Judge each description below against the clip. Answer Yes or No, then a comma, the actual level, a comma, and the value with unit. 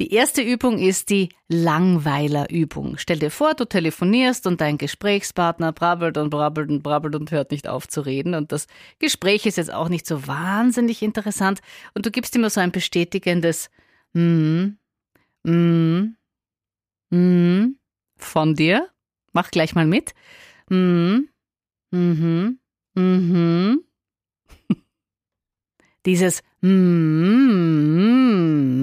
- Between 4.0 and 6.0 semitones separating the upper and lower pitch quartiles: Yes, average, 4.6 semitones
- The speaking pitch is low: No, medium, 175 Hz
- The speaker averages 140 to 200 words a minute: No, slow, 125 wpm